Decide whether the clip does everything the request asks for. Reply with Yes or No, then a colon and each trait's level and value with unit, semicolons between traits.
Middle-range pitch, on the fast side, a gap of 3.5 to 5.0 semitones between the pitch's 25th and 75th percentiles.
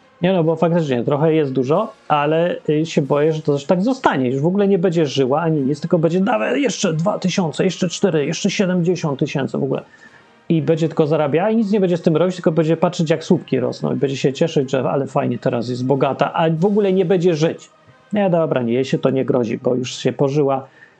Yes: medium, 160 Hz; fast, 235 wpm; average, 4.4 semitones